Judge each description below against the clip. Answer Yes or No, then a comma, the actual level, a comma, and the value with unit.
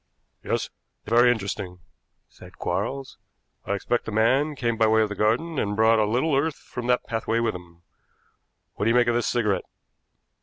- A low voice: Yes, low, 115 Hz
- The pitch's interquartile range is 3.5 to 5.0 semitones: No, narrow, 2.6 semitones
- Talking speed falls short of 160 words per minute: No, average, 185 wpm